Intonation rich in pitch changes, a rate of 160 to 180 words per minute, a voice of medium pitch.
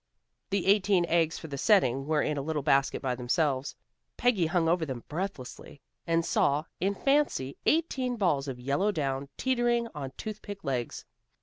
Yes: wide, 6.5 semitones; average, 165 wpm; medium, 165 Hz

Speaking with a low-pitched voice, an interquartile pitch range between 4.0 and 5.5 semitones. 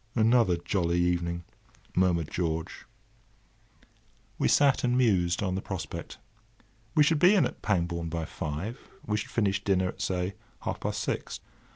Yes: very low, 95 Hz; average, 4.3 semitones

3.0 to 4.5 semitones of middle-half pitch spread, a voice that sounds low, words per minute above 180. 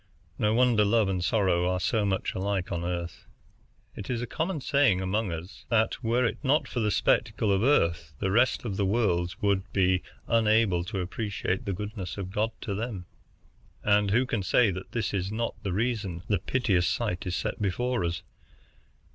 Yes: average, 3.8 semitones; low, 100 Hz; average, 190 wpm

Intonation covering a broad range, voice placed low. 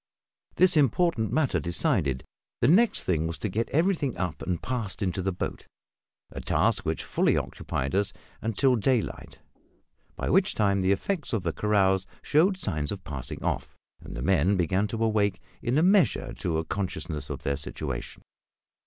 Yes: wide, 6.6 semitones; low, 100 Hz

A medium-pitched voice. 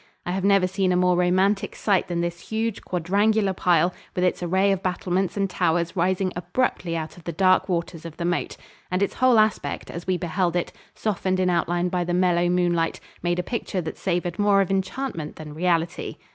Yes: medium, 180 Hz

